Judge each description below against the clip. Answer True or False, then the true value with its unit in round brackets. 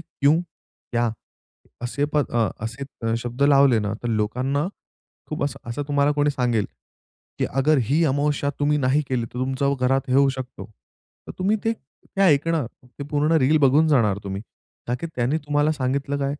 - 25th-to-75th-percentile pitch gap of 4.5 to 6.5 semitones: False (3.0 semitones)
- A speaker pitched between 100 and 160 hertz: True (140 Hz)